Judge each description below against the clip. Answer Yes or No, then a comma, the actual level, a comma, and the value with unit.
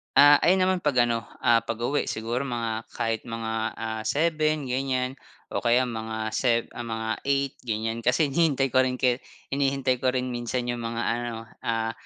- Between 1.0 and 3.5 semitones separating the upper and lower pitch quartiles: Yes, average, 2.9 semitones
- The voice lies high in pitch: No, low, 120 Hz